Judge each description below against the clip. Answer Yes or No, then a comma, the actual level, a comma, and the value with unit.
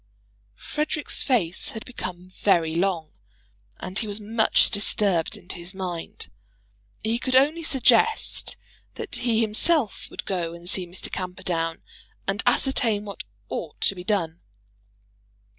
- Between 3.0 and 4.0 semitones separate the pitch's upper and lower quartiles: No, average, 4.7 semitones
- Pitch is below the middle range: No, high, 195 Hz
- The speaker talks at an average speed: No, slow, 130 wpm